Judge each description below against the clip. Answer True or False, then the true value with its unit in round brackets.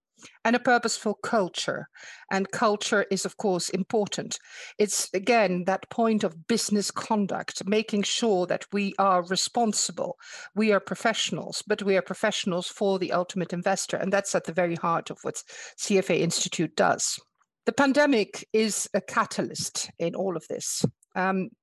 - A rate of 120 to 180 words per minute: True (155 wpm)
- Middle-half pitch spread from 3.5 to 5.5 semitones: False (3.0 semitones)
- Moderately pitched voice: False (200 Hz)